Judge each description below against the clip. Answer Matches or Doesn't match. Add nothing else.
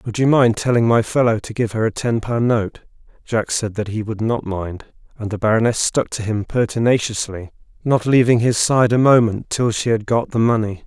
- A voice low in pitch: Matches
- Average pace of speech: Doesn't match